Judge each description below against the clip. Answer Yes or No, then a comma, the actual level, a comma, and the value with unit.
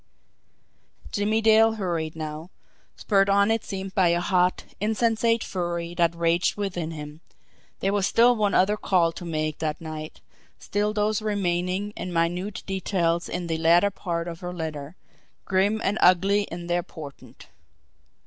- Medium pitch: Yes, medium, 180 Hz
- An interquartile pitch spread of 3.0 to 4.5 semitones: Yes, average, 3.4 semitones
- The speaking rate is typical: Yes, average, 150 wpm